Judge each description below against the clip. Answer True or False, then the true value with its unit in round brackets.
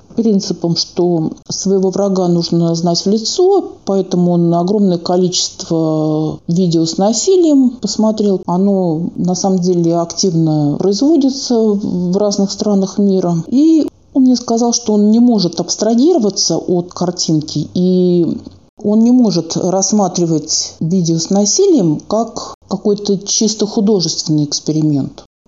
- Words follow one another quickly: False (120 wpm)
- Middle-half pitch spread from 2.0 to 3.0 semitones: False (4.1 semitones)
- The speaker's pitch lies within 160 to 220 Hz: True (190 Hz)